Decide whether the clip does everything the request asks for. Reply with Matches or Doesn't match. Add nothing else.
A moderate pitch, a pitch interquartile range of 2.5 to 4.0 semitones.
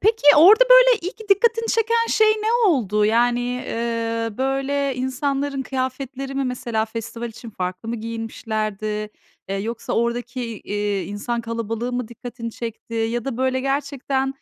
Doesn't match